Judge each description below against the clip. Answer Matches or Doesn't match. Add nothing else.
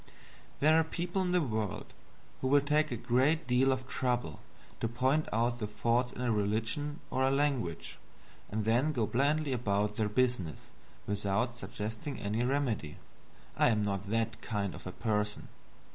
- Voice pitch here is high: Doesn't match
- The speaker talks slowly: Doesn't match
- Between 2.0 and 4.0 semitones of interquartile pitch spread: Doesn't match